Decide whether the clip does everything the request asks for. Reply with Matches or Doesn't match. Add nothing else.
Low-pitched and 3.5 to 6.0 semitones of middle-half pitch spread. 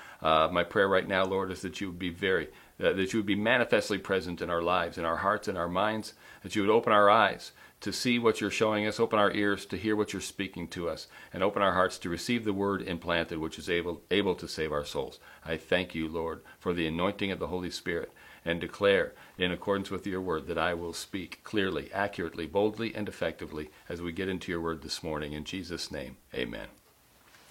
Doesn't match